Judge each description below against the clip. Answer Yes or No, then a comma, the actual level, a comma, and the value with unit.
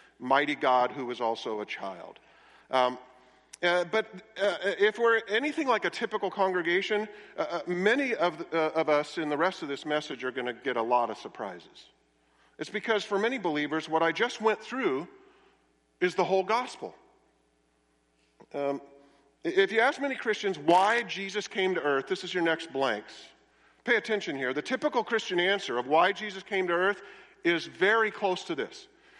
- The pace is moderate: Yes, average, 180 wpm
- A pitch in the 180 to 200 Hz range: Yes, medium, 185 Hz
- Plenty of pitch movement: Yes, wide, 7.3 semitones